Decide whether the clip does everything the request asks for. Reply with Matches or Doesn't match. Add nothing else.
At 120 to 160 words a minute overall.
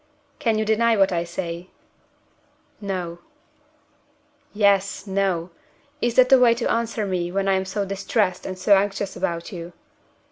Matches